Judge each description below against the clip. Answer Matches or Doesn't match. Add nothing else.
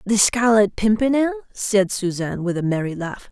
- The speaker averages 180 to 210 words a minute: Doesn't match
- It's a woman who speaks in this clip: Matches